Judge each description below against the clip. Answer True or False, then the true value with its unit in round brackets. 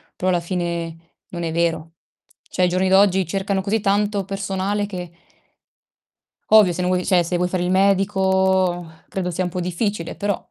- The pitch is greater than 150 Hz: True (185 Hz)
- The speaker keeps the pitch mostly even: True (1.9 semitones)